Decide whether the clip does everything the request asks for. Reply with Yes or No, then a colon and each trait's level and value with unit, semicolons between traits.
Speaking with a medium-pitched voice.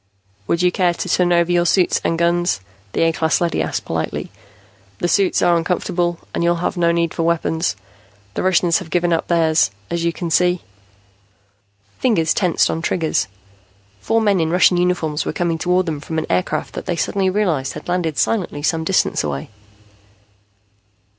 Yes: medium, 170 Hz